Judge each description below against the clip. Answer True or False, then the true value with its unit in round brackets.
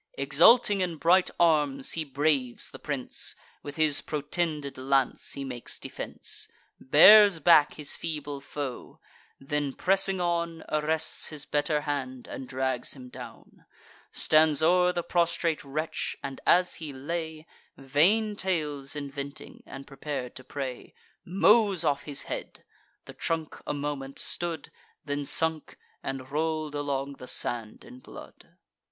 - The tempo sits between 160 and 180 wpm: False (135 wpm)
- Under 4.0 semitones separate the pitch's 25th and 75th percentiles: True (3.3 semitones)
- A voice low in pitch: False (150 Hz)